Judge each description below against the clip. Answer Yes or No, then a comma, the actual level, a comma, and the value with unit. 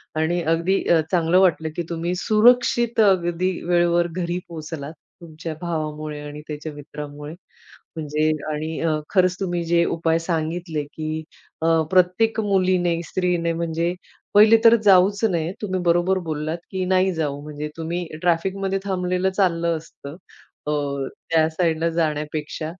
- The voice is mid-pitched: Yes, medium, 170 Hz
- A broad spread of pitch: No, narrow, 2.5 semitones